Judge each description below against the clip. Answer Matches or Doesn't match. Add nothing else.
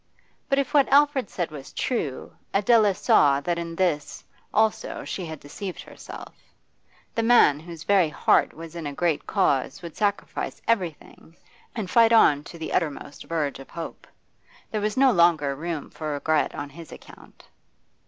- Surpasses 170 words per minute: Doesn't match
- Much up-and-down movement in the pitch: Matches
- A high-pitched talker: Doesn't match